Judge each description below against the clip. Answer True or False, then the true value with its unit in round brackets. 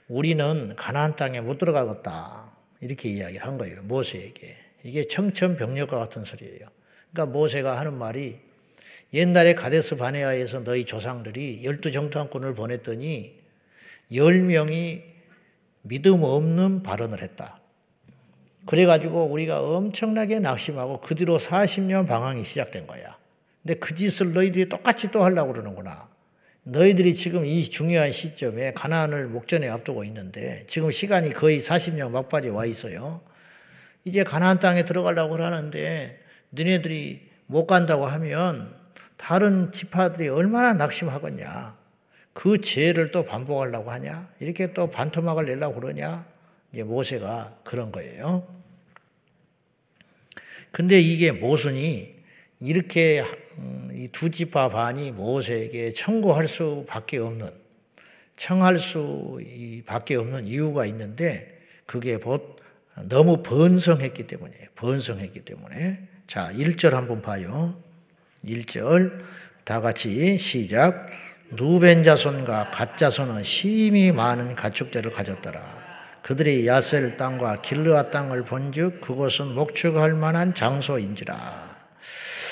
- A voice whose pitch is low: False (155 Hz)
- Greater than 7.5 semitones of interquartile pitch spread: False (5.4 semitones)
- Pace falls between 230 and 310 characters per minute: True (275 characters per minute)